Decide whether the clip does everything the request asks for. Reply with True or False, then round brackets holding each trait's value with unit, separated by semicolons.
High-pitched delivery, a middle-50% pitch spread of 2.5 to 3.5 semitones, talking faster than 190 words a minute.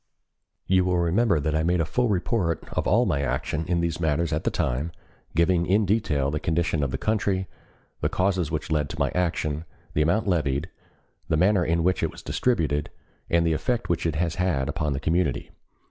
False (85 Hz; 3.2 semitones; 205 wpm)